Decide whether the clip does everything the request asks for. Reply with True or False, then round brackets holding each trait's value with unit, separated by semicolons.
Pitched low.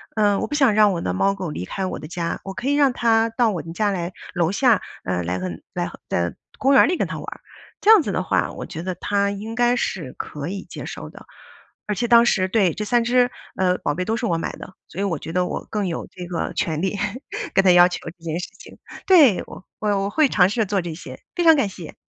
False (195 Hz)